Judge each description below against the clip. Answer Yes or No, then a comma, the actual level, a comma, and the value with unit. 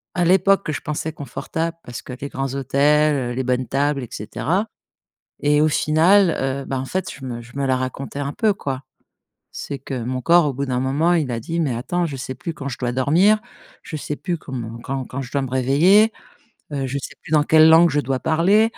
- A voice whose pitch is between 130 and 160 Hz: Yes, medium, 140 Hz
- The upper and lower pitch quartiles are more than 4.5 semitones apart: No, average, 4.0 semitones